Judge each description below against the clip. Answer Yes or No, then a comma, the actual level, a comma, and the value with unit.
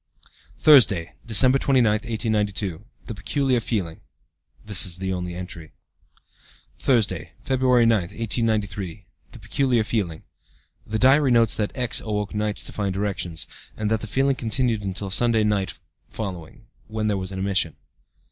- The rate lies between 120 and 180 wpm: Yes, average, 140 wpm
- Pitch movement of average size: Yes, average, 3.6 semitones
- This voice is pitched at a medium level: No, low, 105 Hz